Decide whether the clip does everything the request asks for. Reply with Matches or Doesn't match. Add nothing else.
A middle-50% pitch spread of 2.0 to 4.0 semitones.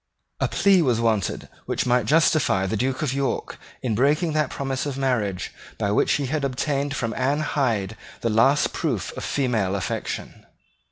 Doesn't match